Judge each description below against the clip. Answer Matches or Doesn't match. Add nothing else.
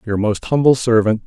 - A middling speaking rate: Matches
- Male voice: Matches